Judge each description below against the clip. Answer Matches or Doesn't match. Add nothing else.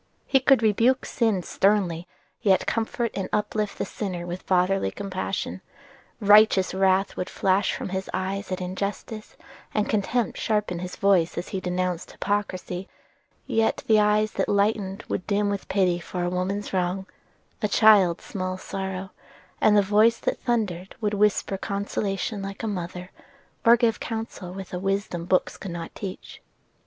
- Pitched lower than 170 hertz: Doesn't match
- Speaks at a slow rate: Doesn't match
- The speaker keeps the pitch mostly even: Matches